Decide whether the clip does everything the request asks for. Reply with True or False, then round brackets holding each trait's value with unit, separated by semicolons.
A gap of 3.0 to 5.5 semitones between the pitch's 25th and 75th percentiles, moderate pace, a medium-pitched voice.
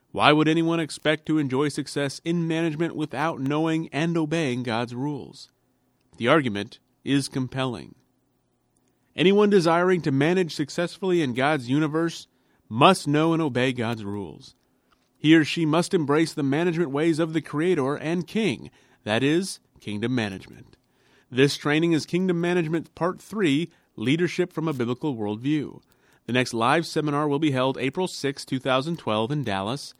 True (4.1 semitones; 150 wpm; 150 Hz)